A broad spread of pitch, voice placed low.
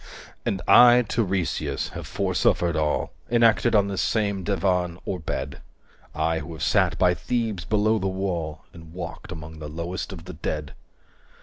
No: average, 3.9 semitones; very low, 90 Hz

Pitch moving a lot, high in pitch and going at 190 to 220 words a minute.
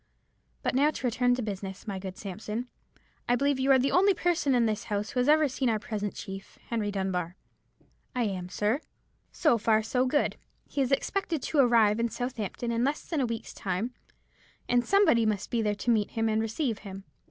No: average, 4.0 semitones; high, 230 Hz; fast, 205 wpm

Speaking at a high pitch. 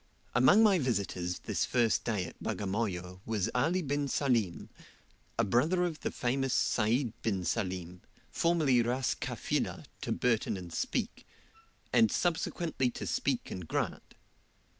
No: low, 120 Hz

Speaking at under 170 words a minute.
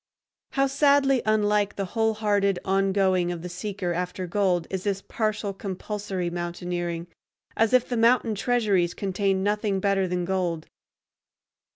Yes: slow, 135 wpm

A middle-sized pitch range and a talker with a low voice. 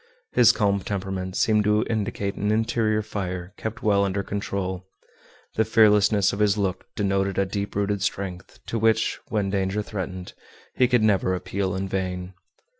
No: narrow, 2.0 semitones; low, 100 Hz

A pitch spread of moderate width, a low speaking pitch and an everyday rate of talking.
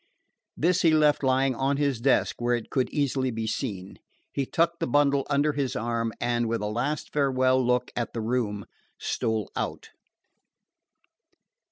Yes: average, 3.3 semitones; low, 130 Hz; average, 160 wpm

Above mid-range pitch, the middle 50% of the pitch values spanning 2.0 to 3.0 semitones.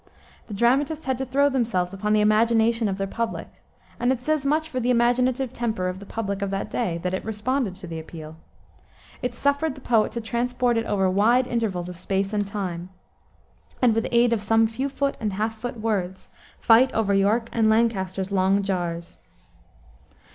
No: high, 225 Hz; average, 3.9 semitones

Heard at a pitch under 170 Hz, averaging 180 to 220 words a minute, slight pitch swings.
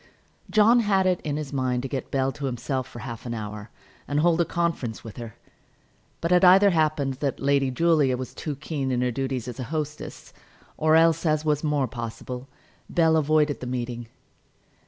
No: medium, 140 Hz; average, 190 wpm; average, 4.1 semitones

